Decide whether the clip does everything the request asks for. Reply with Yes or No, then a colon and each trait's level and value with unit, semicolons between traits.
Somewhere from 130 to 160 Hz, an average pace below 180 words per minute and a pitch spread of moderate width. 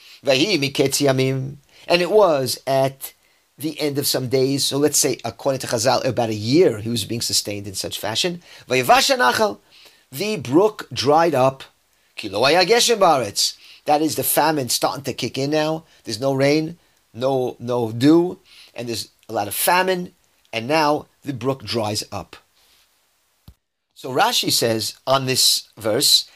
Yes: low, 135 Hz; average, 140 wpm; average, 4.3 semitones